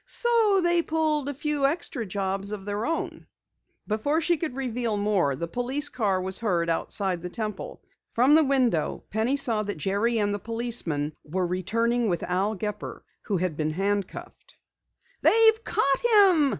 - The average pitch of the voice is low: No, high, 220 Hz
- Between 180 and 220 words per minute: No, average, 165 wpm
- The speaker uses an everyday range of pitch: No, wide, 6.9 semitones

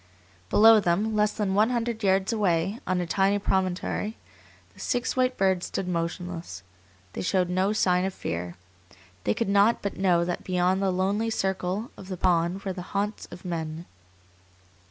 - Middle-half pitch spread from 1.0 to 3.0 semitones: Yes, narrow, 2.6 semitones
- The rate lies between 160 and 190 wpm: Yes, average, 170 wpm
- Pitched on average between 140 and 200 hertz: Yes, high, 190 Hz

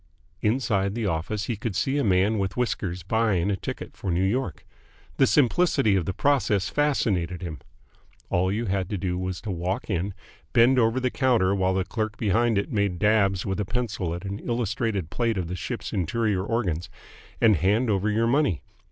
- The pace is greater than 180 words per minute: Yes, average, 190 wpm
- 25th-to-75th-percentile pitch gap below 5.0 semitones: Yes, average, 3.8 semitones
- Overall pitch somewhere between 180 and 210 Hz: No, low, 100 Hz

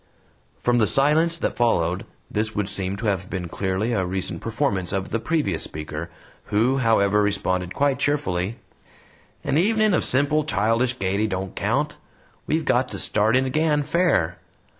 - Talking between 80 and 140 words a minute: No, average, 160 wpm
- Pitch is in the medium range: No, low, 110 Hz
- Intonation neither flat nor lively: No, wide, 6.9 semitones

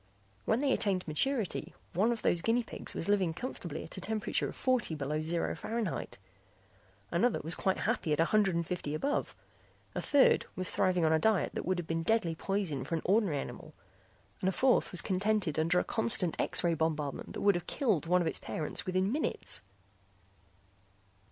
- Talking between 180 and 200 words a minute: Yes, average, 190 wpm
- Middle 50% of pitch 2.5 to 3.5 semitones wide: No, average, 5.0 semitones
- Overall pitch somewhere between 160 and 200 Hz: Yes, medium, 185 Hz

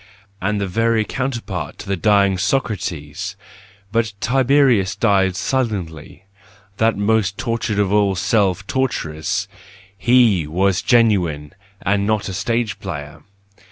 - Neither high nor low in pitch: No, low, 100 Hz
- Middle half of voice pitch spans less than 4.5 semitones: Yes, average, 3.3 semitones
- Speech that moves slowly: Yes, slow, 115 wpm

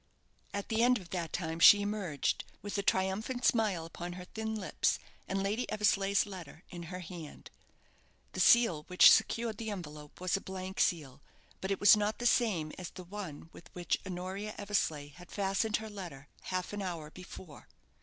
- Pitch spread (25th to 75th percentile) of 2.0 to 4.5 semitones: Yes, average, 3.3 semitones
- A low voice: No, high, 190 Hz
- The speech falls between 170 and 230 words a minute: Yes, average, 180 wpm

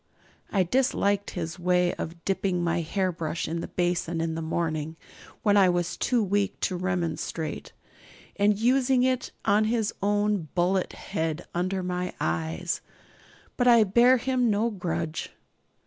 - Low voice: No, medium, 185 Hz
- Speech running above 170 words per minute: No, average, 145 wpm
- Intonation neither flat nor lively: Yes, average, 3.6 semitones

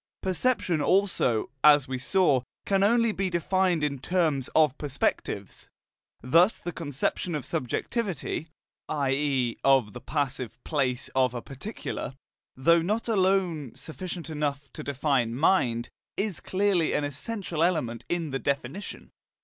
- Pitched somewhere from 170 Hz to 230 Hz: No, medium, 150 Hz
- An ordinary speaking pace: No, slow, 125 wpm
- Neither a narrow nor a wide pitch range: No, wide, 5.7 semitones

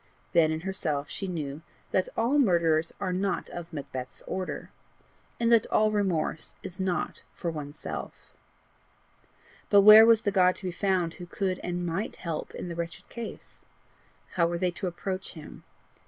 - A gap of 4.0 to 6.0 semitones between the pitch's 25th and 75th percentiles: No, average, 2.8 semitones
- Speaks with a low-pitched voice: No, medium, 180 Hz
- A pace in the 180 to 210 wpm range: No, average, 165 wpm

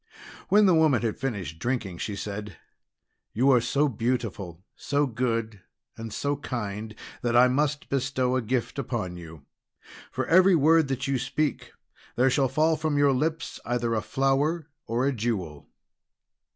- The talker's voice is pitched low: Yes, low, 125 Hz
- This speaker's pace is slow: No, average, 155 wpm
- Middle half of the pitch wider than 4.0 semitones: Yes, average, 4.7 semitones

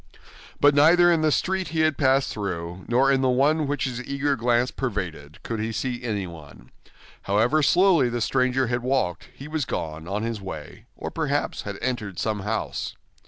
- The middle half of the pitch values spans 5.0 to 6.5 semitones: Yes, wide, 5.6 semitones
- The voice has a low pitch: Yes, low, 125 Hz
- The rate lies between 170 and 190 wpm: Yes, average, 180 wpm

